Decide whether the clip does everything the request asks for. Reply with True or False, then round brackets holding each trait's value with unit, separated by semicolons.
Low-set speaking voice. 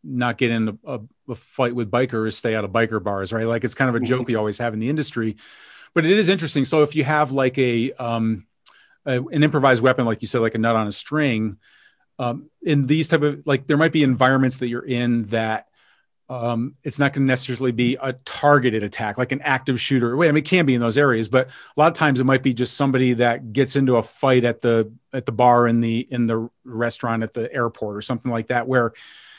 True (125 Hz)